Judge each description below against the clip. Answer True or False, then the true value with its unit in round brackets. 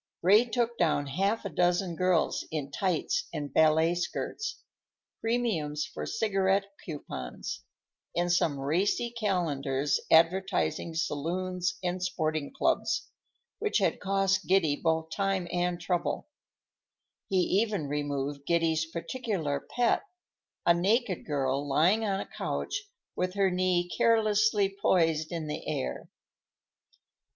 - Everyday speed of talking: False (115 wpm)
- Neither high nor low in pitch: True (175 Hz)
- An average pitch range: True (4.0 semitones)